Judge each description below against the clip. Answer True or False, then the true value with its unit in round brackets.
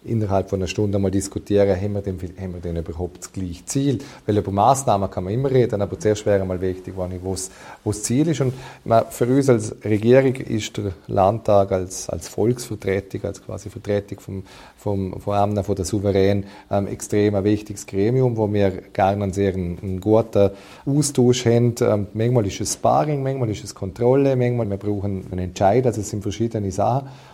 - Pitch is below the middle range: True (100 Hz)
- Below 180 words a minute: False (190 wpm)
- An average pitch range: True (3.2 semitones)